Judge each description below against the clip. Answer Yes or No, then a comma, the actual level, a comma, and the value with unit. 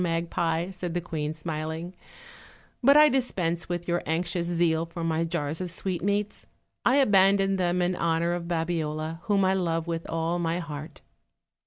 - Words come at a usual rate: Yes, average, 160 wpm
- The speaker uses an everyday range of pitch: No, narrow, 1.8 semitones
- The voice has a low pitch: No, medium, 170 Hz